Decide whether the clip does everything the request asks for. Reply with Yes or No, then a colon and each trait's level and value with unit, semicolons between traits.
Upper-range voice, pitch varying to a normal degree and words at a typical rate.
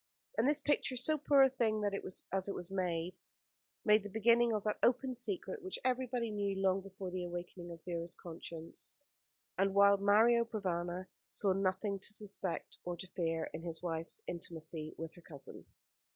Yes: high, 195 Hz; average, 4.6 semitones; average, 165 wpm